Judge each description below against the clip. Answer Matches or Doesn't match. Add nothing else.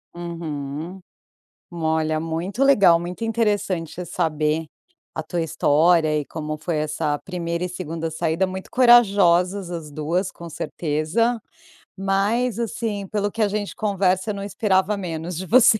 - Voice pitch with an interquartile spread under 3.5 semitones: Doesn't match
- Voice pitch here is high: Doesn't match